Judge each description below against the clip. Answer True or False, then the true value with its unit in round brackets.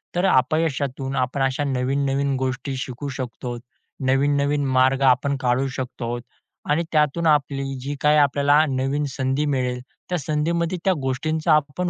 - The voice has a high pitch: False (140 Hz)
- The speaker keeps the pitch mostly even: True (2.3 semitones)